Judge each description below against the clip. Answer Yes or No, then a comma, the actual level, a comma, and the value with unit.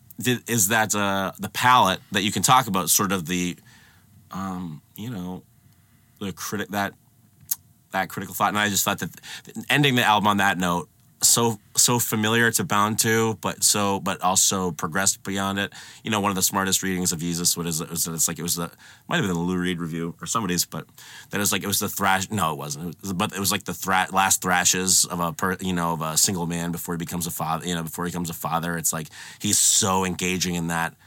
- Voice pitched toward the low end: Yes, very low, 95 Hz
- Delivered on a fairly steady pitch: No, average, 3.3 semitones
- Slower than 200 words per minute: No, fast, 240 wpm